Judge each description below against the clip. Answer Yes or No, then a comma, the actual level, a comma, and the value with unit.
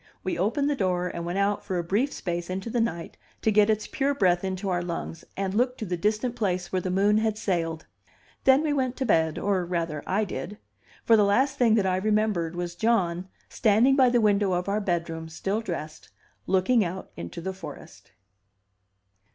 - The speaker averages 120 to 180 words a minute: No, average, 200 wpm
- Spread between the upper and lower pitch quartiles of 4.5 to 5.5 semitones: No, average, 3.9 semitones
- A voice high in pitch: Yes, high, 195 Hz